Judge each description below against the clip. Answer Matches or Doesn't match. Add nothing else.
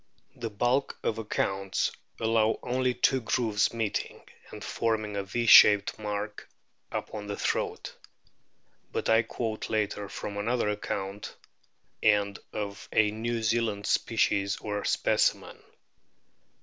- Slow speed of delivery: Matches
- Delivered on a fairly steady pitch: Matches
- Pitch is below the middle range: Matches